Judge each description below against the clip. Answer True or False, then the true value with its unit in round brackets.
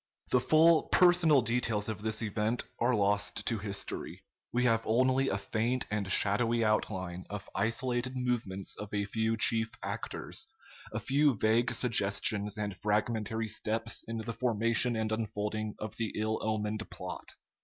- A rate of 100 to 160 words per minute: True (150 wpm)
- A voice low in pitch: True (110 Hz)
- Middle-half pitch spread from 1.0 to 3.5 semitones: True (2.4 semitones)